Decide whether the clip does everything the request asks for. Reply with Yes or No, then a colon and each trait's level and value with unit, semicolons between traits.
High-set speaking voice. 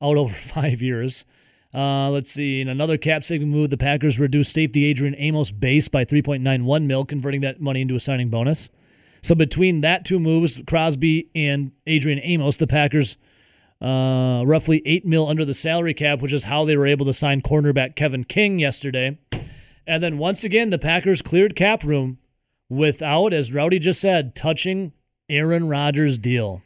No: medium, 145 Hz